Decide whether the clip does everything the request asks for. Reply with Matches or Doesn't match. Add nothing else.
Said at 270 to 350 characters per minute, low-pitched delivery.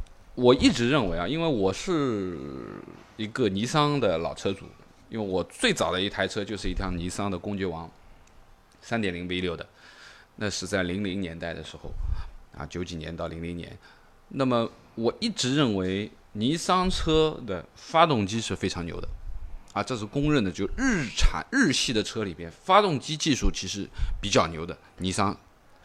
Doesn't match